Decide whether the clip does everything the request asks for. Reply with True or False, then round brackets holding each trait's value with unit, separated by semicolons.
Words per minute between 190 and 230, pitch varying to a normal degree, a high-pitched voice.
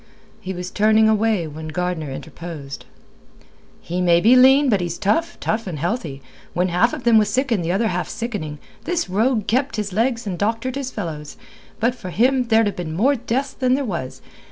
False (195 wpm; 5.9 semitones; 210 Hz)